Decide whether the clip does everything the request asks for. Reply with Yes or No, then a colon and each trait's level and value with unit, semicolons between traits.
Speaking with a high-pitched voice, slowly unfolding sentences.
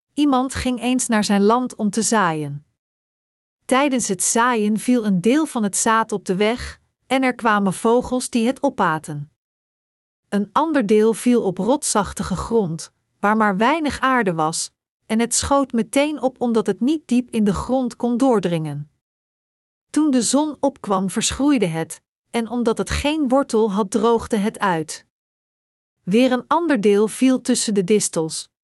No: high, 230 Hz; average, 160 wpm